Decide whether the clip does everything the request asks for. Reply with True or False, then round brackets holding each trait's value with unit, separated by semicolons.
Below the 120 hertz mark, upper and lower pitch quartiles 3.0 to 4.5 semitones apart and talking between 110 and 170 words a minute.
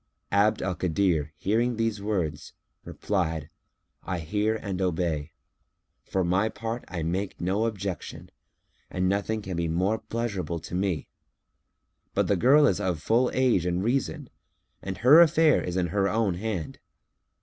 True (95 Hz; 4.0 semitones; 150 wpm)